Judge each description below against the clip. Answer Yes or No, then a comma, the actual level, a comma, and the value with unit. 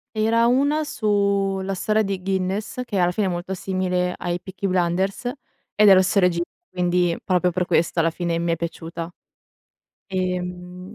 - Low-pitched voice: No, medium, 185 Hz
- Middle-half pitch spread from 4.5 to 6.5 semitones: No, narrow, 2.0 semitones